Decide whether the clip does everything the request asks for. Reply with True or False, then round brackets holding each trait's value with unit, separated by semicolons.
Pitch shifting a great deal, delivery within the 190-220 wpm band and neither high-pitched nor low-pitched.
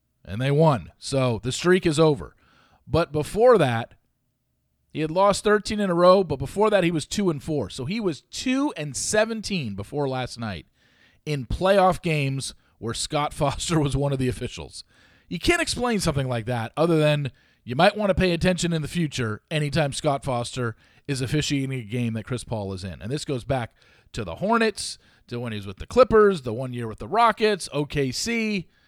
True (7.1 semitones; 200 wpm; 145 Hz)